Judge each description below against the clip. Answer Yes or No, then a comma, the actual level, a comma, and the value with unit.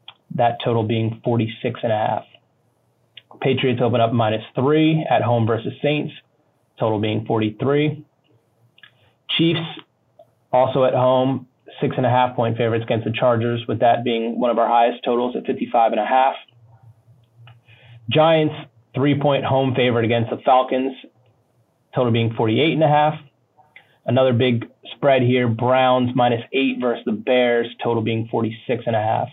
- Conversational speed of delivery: Yes, average, 155 wpm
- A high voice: No, low, 125 Hz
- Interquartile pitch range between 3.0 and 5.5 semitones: No, narrow, 2.4 semitones